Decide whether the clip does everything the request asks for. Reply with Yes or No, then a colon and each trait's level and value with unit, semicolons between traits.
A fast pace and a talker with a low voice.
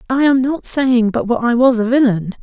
No: fast, 245 wpm; high, 245 Hz